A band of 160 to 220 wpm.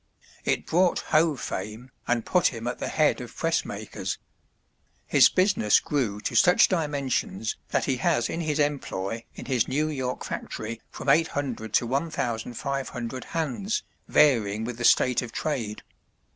No: average, 150 wpm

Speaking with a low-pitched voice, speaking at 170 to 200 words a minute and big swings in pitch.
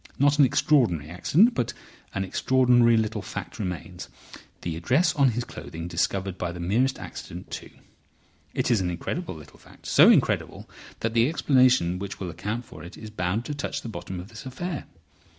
Yes: low, 110 Hz; average, 180 wpm; wide, 6.5 semitones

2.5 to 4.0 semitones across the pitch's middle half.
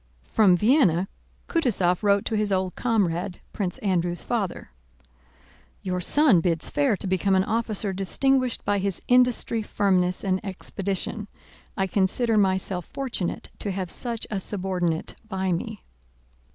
Yes: average, 3.3 semitones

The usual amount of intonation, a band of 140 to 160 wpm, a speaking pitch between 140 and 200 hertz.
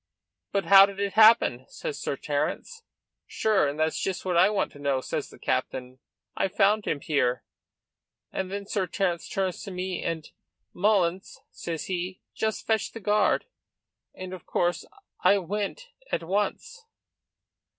Yes: average, 3.5 semitones; average, 155 wpm; high, 190 Hz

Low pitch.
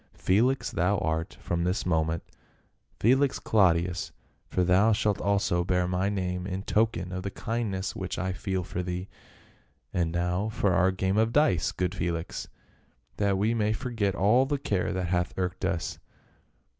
Yes: very low, 95 Hz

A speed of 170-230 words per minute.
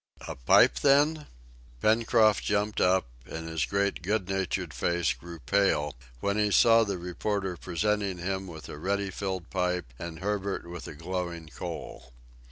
No: average, 155 wpm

